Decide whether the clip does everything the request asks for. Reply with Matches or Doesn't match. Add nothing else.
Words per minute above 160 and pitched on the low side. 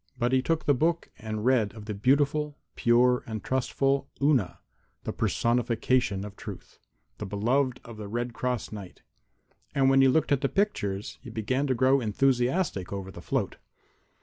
Matches